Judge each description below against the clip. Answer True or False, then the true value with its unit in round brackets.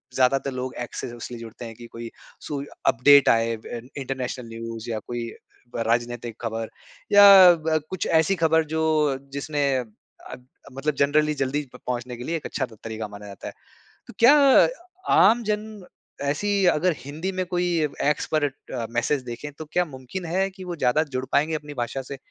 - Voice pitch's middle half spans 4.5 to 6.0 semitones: True (5.0 semitones)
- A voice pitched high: False (140 Hz)